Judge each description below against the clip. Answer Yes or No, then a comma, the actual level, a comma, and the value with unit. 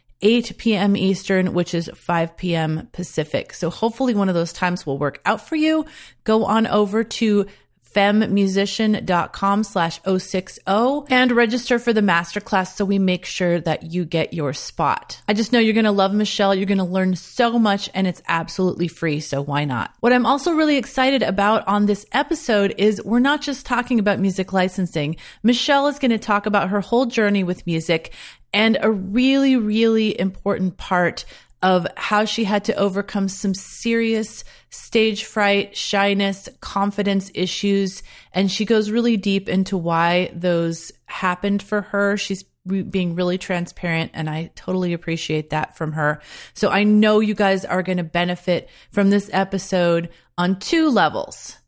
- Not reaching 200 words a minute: Yes, average, 170 wpm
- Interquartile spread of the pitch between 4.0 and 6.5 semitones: No, average, 3.5 semitones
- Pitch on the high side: Yes, high, 200 Hz